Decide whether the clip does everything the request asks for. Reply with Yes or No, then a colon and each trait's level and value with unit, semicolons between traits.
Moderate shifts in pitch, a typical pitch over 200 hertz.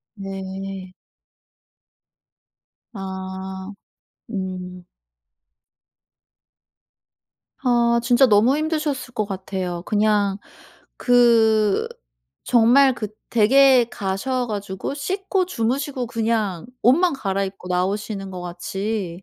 Yes: average, 4.4 semitones; high, 210 Hz